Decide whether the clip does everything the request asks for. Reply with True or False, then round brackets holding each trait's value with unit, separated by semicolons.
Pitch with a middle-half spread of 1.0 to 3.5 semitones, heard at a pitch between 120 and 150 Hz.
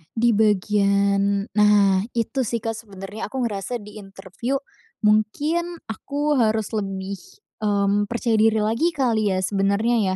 False (2.6 semitones; 210 Hz)